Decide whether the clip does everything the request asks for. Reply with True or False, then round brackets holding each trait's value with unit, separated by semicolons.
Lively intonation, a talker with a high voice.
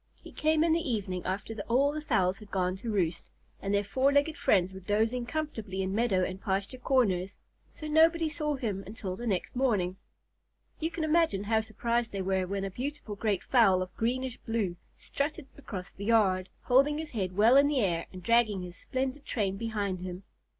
True (5.7 semitones; 220 Hz)